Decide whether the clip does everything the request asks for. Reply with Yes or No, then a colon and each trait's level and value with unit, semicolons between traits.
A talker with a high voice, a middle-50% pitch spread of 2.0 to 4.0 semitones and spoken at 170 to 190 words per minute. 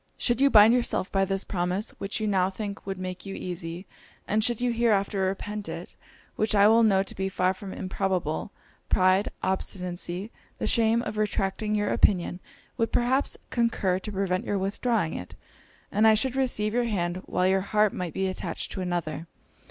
Yes: high, 195 Hz; average, 2.8 semitones; average, 180 wpm